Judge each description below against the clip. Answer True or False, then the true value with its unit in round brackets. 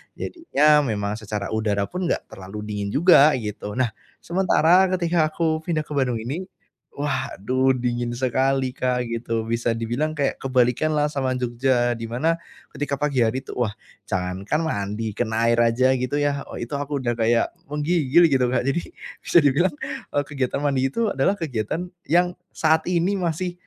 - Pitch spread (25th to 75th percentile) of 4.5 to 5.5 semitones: True (4.8 semitones)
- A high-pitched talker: False (130 Hz)